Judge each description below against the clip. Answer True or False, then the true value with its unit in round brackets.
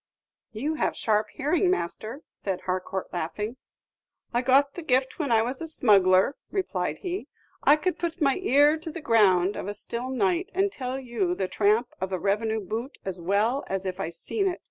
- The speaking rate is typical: True (190 wpm)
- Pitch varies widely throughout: True (7.0 semitones)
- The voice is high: True (235 Hz)